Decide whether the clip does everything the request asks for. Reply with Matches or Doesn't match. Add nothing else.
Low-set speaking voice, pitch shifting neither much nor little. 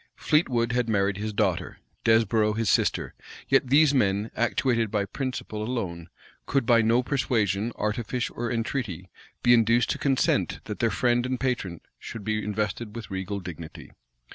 Matches